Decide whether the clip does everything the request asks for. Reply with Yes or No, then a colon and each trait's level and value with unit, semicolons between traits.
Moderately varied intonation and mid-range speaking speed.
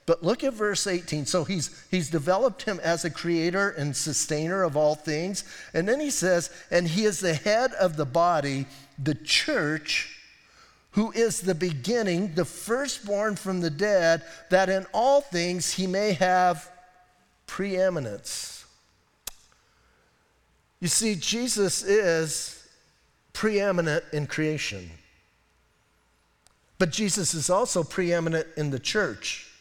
No: average, 4.1 semitones; slow, 130 wpm